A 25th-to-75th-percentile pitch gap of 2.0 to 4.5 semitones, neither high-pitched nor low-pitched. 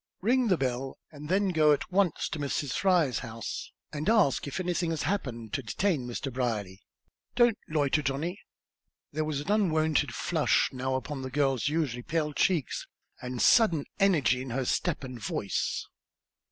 No: average, 5.2 semitones; medium, 145 Hz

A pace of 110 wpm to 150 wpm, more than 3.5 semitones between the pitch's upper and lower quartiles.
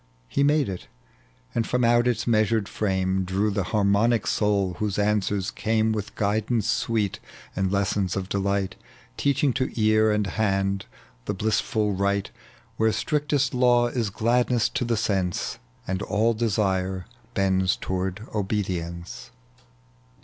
No: slow, 135 wpm; average, 2.9 semitones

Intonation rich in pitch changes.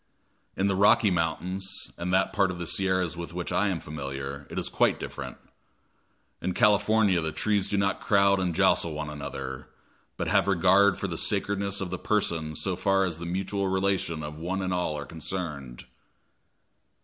No: average, 3.5 semitones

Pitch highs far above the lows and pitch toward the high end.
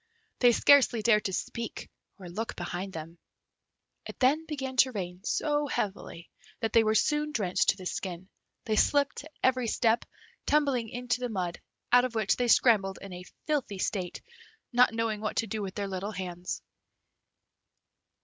No: average, 4.9 semitones; high, 225 Hz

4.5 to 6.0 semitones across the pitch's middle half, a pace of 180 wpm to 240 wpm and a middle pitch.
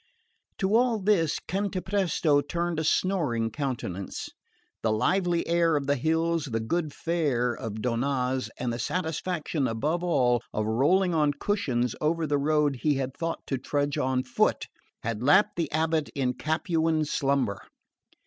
No: average, 5.0 semitones; average, 150 wpm; medium, 150 Hz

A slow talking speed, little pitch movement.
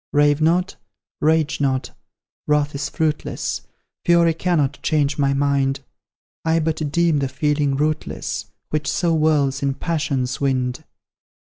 Yes: slow, 125 wpm; narrow, 2.3 semitones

